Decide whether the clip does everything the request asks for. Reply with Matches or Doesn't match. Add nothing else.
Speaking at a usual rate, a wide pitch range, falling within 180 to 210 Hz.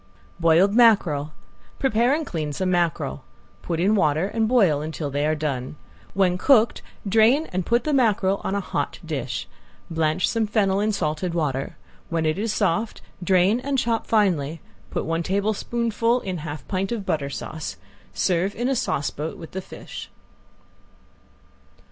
Matches